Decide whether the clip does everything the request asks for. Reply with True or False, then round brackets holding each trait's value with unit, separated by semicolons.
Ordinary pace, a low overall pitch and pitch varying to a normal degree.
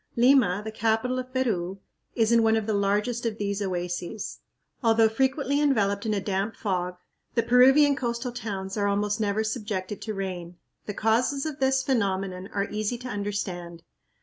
False (170 wpm; 215 Hz; 3.7 semitones)